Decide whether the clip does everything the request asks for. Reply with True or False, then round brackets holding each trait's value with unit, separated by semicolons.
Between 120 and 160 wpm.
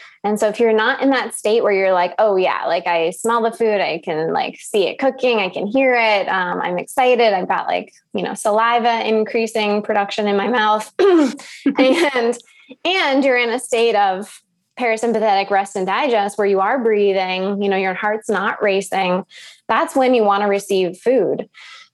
False (190 wpm)